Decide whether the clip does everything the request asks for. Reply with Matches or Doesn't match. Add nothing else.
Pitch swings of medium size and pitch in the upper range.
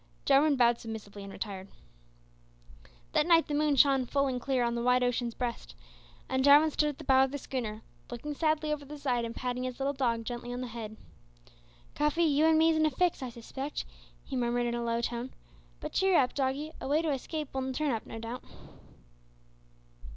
Matches